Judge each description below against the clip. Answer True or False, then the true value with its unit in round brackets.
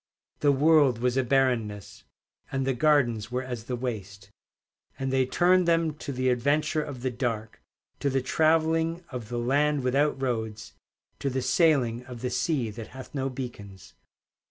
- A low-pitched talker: True (130 Hz)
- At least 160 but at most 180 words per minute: True (165 wpm)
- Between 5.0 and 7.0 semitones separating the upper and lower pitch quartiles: False (3.3 semitones)